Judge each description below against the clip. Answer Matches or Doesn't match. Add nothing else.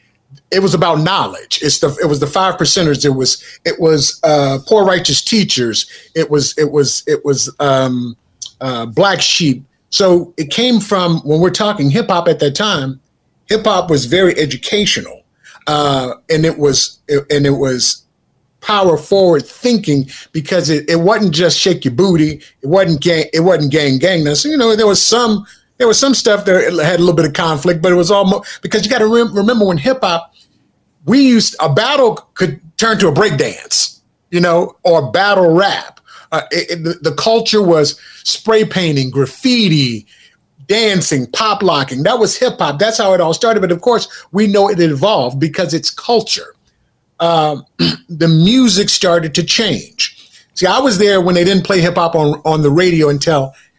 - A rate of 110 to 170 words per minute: Doesn't match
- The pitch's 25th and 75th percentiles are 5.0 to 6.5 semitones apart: Matches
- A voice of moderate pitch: Matches